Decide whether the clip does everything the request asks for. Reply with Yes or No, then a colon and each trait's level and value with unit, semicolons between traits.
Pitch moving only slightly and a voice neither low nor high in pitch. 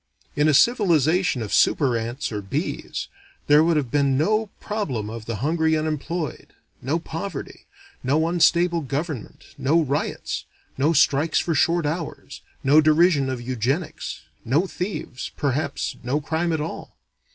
No: average, 3.9 semitones; medium, 155 Hz